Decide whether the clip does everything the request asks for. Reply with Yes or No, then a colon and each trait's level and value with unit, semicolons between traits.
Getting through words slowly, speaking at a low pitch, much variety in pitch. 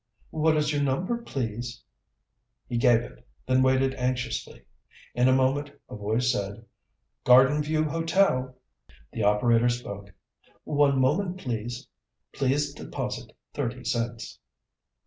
No: slow, 120 wpm; low, 130 Hz; average, 3.5 semitones